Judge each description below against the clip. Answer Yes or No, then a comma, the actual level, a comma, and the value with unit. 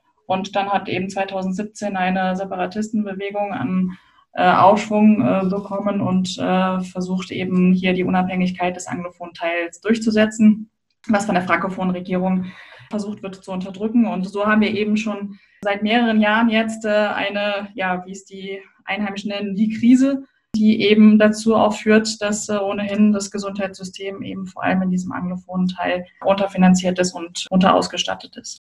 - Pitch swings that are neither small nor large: No, narrow, 2.3 semitones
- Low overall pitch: No, high, 195 Hz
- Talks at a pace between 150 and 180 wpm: Yes, average, 155 wpm